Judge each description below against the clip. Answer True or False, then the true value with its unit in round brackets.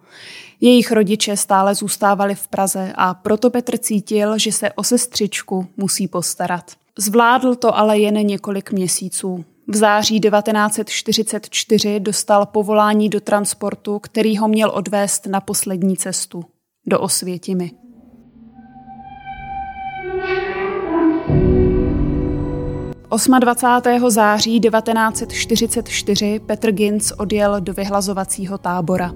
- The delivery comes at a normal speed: False (95 wpm)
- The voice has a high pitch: True (210 Hz)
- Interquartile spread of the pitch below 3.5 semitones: True (2.8 semitones)